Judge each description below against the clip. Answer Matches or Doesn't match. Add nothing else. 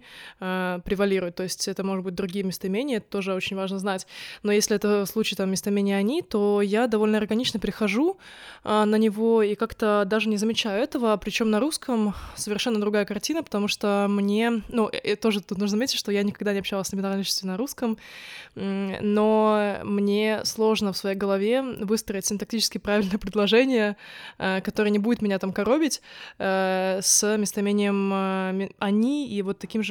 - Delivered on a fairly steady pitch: Matches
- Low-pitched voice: Doesn't match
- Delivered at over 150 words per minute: Matches